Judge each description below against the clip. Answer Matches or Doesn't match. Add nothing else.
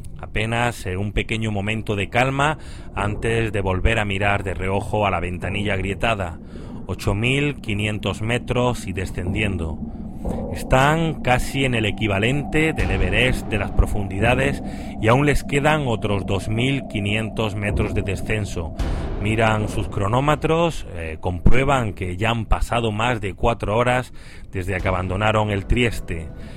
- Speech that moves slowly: Matches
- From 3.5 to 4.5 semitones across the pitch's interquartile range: Matches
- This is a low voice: Matches